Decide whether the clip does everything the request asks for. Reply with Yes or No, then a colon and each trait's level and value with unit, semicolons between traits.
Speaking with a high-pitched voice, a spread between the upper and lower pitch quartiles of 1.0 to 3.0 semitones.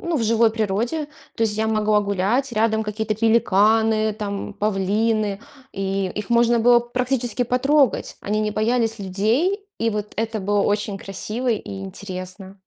Yes: high, 215 Hz; narrow, 2.6 semitones